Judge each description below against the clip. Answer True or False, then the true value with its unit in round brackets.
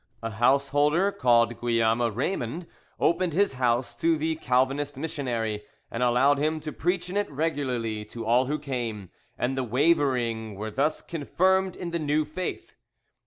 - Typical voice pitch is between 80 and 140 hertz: True (135 Hz)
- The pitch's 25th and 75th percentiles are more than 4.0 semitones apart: True (5.1 semitones)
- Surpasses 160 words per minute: False (155 wpm)